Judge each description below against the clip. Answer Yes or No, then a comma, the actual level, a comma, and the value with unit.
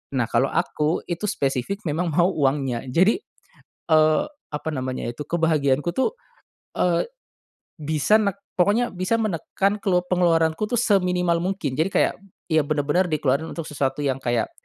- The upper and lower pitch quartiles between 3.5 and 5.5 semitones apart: Yes, average, 4.3 semitones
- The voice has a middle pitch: Yes, medium, 160 Hz